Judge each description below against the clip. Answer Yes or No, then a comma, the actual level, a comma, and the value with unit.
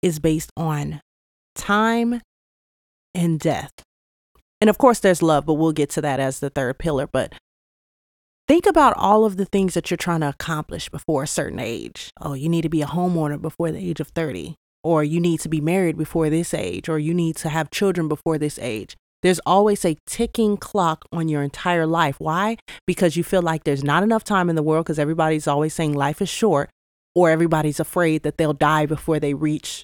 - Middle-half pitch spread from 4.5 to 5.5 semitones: No, average, 2.8 semitones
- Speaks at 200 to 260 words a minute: Yes, fast, 205 wpm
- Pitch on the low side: No, medium, 160 Hz